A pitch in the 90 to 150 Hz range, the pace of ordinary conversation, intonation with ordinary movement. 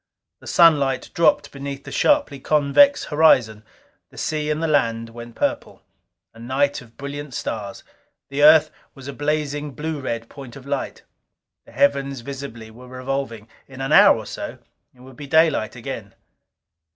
Yes: medium, 140 Hz; average, 160 wpm; average, 3.3 semitones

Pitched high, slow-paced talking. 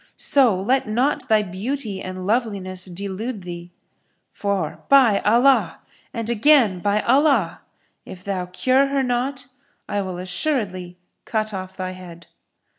Yes: high, 205 Hz; slow, 130 wpm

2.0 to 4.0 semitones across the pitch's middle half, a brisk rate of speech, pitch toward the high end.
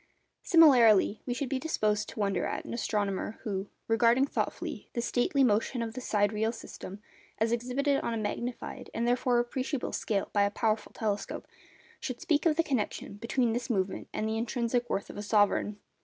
No: average, 3.1 semitones; average, 180 wpm; high, 230 Hz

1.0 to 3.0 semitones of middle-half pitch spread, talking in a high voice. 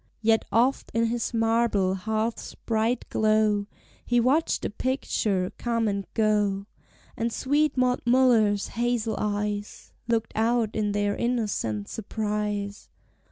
Yes: narrow, 2.4 semitones; high, 220 Hz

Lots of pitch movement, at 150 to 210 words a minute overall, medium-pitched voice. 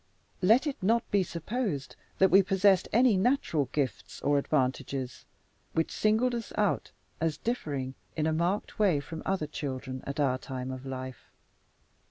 Yes: wide, 7.4 semitones; average, 155 wpm; medium, 160 Hz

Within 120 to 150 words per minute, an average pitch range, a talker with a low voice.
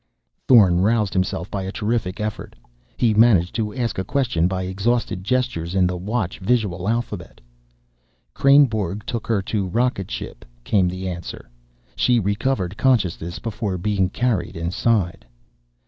Yes: average, 140 wpm; average, 4.2 semitones; low, 100 Hz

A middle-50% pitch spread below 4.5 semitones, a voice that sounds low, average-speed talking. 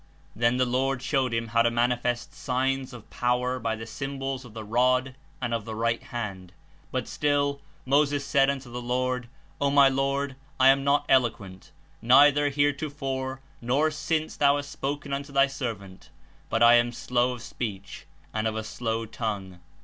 Yes: average, 2.9 semitones; low, 125 Hz; average, 175 wpm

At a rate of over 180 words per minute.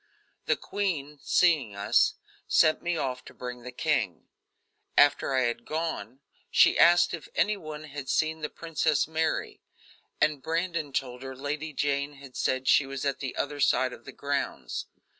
No: average, 165 wpm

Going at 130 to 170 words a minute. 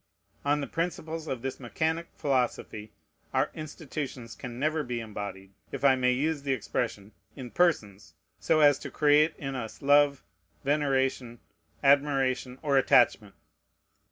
Yes: slow, 135 wpm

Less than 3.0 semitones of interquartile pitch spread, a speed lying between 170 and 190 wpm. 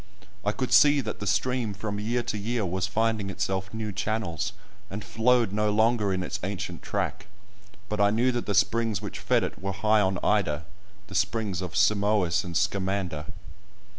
Yes: narrow, 2.4 semitones; average, 175 wpm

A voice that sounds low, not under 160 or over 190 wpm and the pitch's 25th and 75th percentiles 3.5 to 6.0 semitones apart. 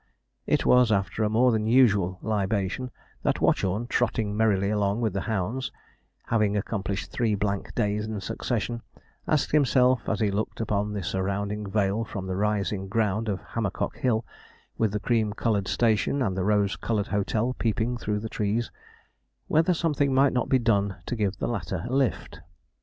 No: low, 105 Hz; average, 170 wpm; average, 2.7 semitones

